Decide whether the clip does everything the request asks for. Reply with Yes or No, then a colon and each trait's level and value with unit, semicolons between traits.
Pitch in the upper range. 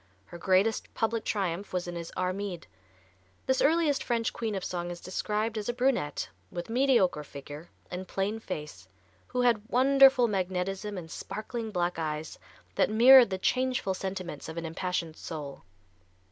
Yes: high, 195 Hz